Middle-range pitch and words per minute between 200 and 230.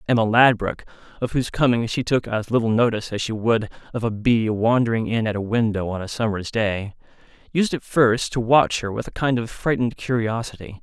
No: low, 115 Hz; fast, 205 wpm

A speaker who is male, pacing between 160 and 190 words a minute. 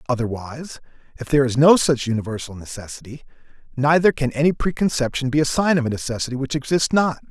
Yes: male; average, 170 wpm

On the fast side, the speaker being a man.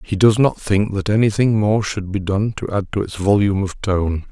Yes: fast, 235 wpm; male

